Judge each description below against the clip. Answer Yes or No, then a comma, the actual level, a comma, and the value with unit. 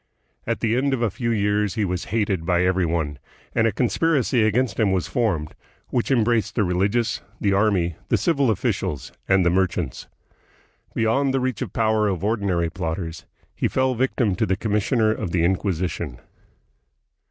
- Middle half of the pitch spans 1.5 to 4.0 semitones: No, average, 4.4 semitones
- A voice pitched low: Yes, low, 105 Hz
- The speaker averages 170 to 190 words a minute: Yes, average, 180 wpm